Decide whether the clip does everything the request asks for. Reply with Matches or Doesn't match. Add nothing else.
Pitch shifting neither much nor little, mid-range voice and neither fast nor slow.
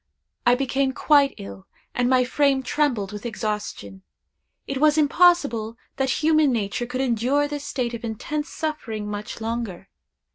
Doesn't match